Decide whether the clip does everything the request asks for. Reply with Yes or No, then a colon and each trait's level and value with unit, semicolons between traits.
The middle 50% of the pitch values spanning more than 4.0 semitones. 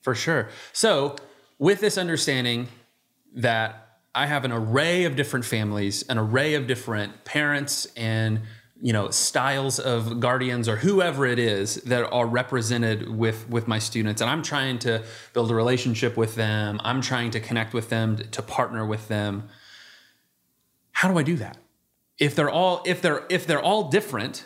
Yes: average, 4.4 semitones